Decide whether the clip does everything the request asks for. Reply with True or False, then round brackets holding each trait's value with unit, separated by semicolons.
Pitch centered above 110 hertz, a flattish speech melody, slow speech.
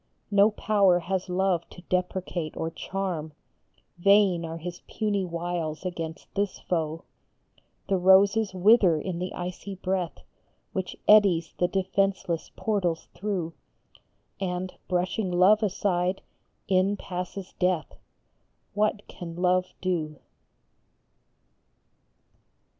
True (185 Hz; 2.1 semitones; 105 wpm)